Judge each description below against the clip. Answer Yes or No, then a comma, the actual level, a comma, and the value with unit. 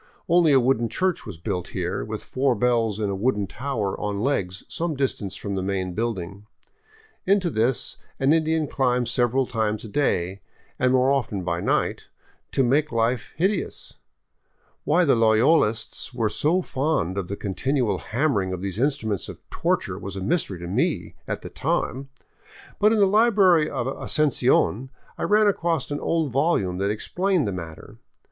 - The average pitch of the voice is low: Yes, low, 125 Hz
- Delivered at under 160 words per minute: No, average, 165 wpm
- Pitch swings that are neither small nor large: No, wide, 7.0 semitones